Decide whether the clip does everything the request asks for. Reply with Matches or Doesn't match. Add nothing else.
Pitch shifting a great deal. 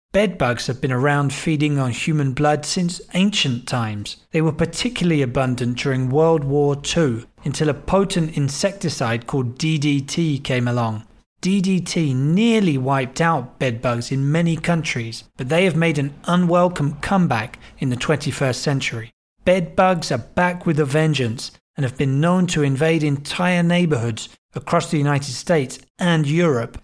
Doesn't match